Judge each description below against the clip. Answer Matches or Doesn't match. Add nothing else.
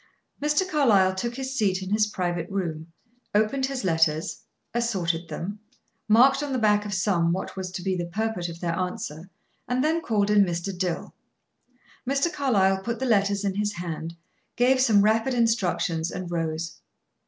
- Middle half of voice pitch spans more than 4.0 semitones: Matches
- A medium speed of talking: Matches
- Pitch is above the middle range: Matches